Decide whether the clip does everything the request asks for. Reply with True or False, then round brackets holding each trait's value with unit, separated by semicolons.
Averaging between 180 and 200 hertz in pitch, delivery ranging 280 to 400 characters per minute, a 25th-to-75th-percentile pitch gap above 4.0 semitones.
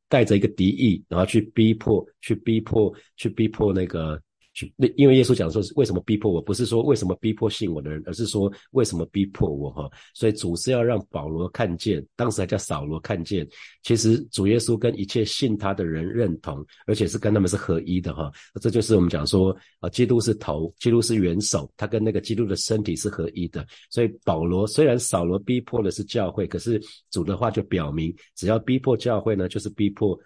False (105 Hz; 315 characters per minute; 4.4 semitones)